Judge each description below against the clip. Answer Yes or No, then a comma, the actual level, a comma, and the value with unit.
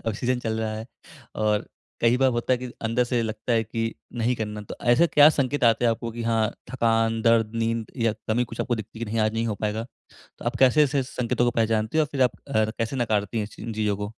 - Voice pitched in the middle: No, low, 115 Hz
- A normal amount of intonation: No, narrow, 1.9 semitones